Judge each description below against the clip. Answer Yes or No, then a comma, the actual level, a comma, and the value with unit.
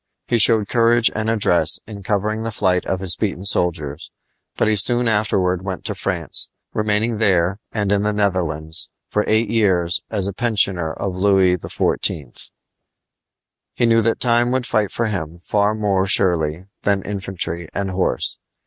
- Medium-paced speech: Yes, average, 160 wpm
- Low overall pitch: Yes, low, 100 Hz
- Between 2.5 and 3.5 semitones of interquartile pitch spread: Yes, average, 3.1 semitones